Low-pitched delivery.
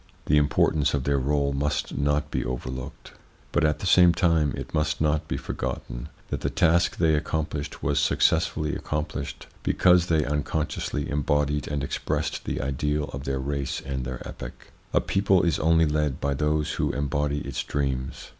Yes: very low, 75 Hz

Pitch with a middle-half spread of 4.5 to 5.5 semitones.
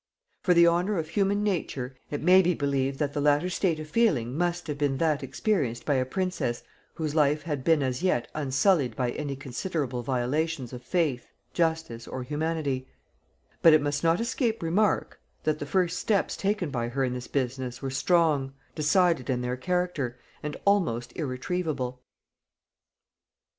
Yes: average, 5.0 semitones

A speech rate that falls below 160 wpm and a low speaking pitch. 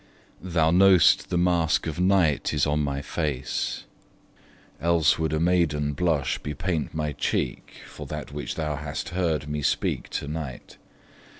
Yes: average, 145 wpm; very low, 80 Hz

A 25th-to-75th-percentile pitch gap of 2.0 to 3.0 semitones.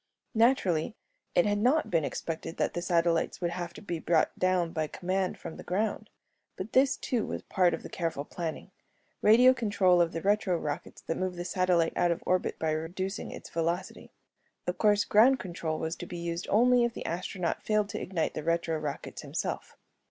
No: average, 3.7 semitones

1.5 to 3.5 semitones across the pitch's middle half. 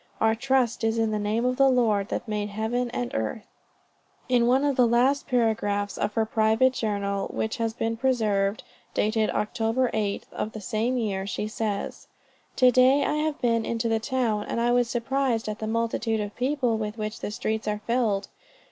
Yes: narrow, 2.6 semitones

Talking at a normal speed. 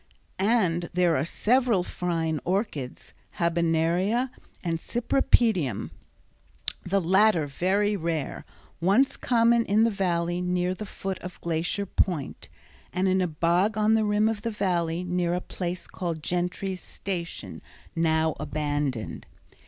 No: slow, 130 wpm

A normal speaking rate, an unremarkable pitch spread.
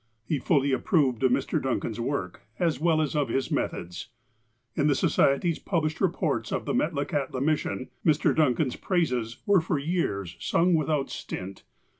Yes: average, 160 wpm; average, 4.1 semitones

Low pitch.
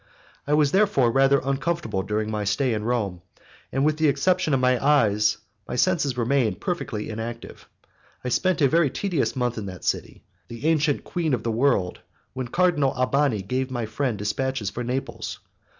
Yes: low, 130 Hz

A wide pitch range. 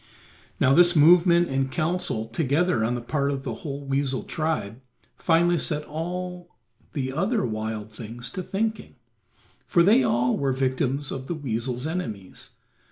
Yes: wide, 5.7 semitones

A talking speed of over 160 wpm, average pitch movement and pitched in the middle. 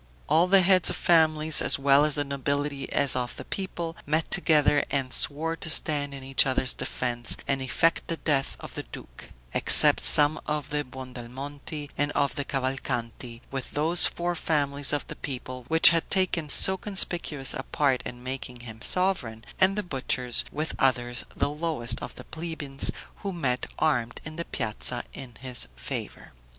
Yes: average, 175 wpm; average, 3.8 semitones; medium, 145 Hz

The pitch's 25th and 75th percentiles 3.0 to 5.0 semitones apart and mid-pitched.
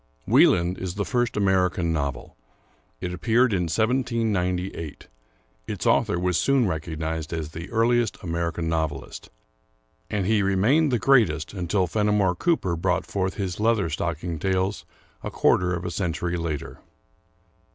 No: average, 4.0 semitones; very low, 90 Hz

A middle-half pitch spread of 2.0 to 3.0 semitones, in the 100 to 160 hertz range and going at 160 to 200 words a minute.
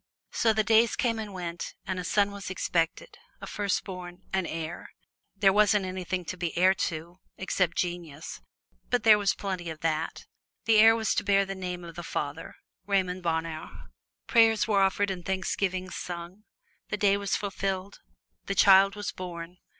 No: average, 2.7 semitones; high, 190 Hz; average, 170 wpm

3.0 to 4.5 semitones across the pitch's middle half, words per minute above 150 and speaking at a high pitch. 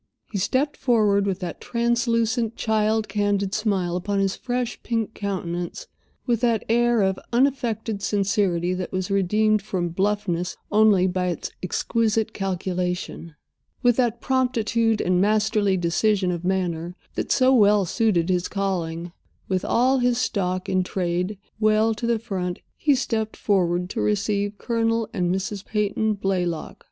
No: average, 3.6 semitones; average, 140 wpm; high, 205 Hz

